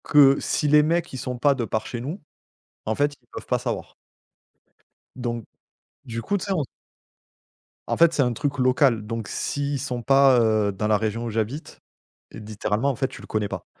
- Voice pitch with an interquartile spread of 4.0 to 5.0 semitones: Yes, average, 4.4 semitones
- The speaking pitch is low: Yes, low, 125 Hz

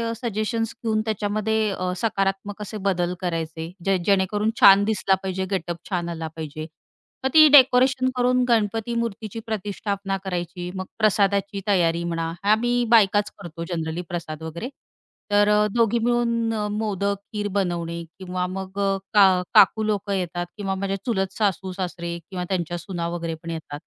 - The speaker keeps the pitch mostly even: No, average, 3.5 semitones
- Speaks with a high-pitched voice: Yes, high, 195 Hz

